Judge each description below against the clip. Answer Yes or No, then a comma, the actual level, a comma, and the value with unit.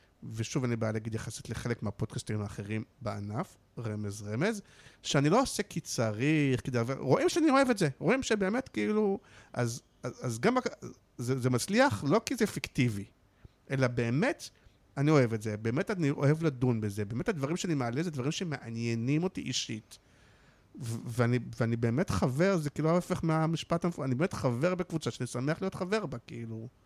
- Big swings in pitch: Yes, wide, 6.6 semitones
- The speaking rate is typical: No, fast, 170 wpm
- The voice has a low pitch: Yes, low, 130 Hz